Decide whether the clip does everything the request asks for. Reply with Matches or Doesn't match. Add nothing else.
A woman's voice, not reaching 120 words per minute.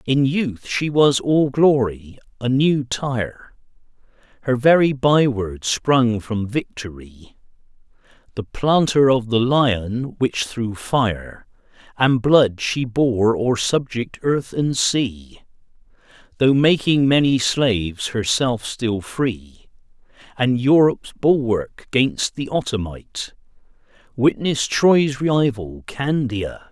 Doesn't match